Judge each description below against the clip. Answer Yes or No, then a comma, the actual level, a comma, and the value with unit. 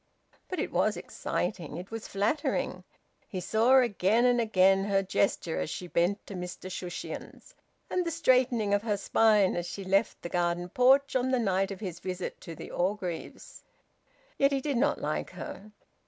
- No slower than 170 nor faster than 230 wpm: Yes, average, 175 wpm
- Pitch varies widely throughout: No, average, 5.0 semitones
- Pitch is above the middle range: Yes, high, 200 Hz